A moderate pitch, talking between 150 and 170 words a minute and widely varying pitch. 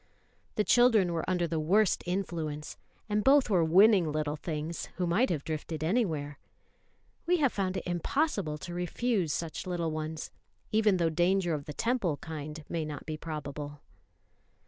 No: medium, 170 Hz; average, 160 wpm; average, 4.4 semitones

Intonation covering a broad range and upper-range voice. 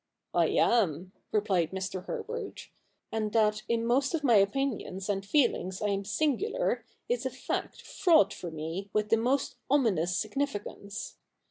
No: average, 5.0 semitones; high, 210 Hz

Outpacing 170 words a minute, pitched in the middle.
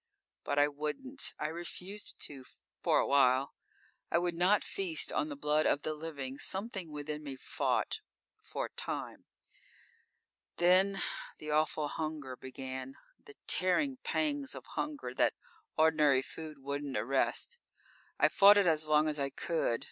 No: average, 150 wpm; medium, 155 Hz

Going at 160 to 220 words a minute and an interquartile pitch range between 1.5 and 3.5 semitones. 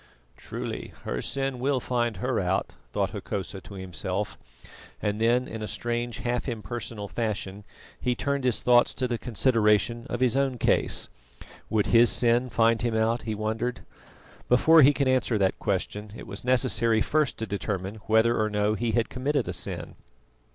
Yes: average, 170 wpm; average, 2.9 semitones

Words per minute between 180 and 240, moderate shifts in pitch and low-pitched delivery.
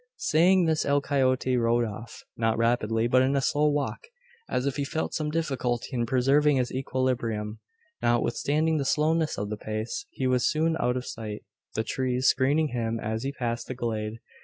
Yes: average, 185 wpm; average, 3.8 semitones; low, 130 Hz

